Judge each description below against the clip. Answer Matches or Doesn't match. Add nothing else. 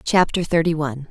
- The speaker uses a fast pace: Doesn't match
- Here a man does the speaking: Doesn't match